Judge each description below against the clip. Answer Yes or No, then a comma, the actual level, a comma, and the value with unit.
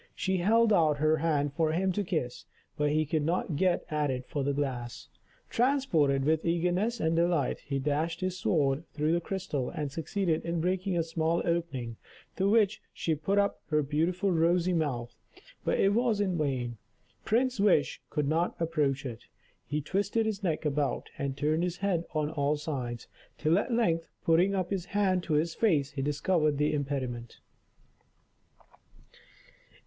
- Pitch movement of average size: Yes, average, 4.2 semitones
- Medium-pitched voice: Yes, medium, 160 Hz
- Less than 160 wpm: No, average, 170 wpm